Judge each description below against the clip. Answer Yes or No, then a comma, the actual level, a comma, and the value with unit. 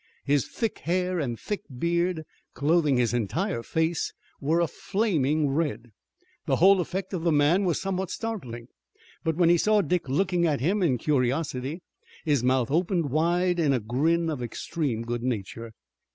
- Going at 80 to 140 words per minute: No, average, 165 wpm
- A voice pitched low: No, medium, 160 Hz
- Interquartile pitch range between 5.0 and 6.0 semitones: Yes, average, 5.3 semitones